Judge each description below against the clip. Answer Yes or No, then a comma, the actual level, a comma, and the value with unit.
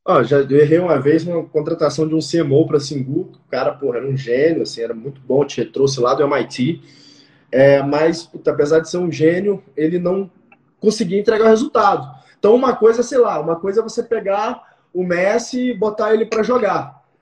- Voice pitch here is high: No, medium, 165 Hz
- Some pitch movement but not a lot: No, wide, 6.9 semitones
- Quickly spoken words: Yes, fast, 205 wpm